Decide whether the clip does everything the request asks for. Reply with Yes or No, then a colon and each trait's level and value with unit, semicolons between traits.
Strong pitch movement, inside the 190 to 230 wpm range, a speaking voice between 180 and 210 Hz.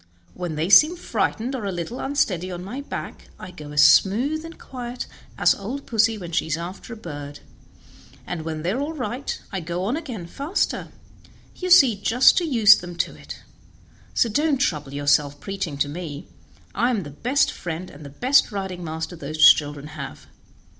Yes: wide, 7.8 semitones; average, 195 wpm; high, 190 Hz